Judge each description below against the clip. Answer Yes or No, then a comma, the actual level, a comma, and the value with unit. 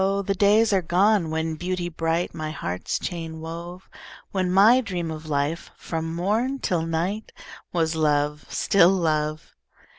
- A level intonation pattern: No, average, 3.3 semitones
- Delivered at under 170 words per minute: Yes, average, 145 wpm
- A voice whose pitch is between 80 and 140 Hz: No, medium, 170 Hz